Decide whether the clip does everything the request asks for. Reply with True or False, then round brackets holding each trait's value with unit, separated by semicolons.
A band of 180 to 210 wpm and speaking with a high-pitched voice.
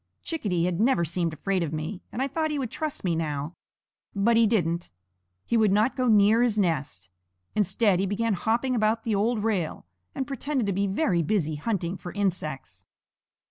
True (185 wpm; 200 Hz)